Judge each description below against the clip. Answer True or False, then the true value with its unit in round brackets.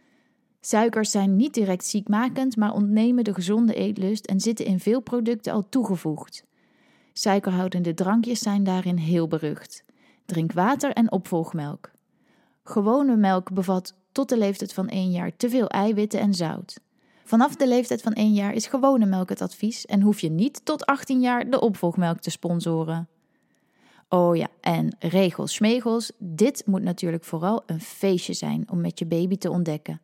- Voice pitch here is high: True (205 Hz)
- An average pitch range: True (4.4 semitones)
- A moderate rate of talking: True (160 wpm)